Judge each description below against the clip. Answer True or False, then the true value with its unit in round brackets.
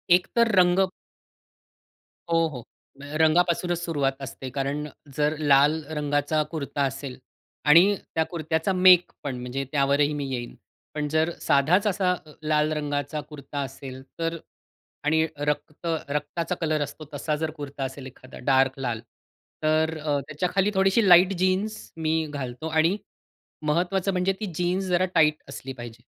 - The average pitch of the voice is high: False (155 Hz)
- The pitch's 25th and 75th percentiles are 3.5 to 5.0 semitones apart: True (3.8 semitones)